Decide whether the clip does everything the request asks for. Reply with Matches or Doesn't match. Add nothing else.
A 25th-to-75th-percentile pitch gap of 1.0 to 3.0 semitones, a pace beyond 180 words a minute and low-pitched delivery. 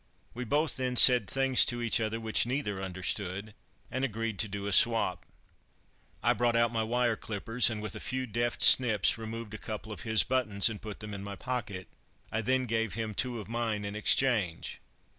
Matches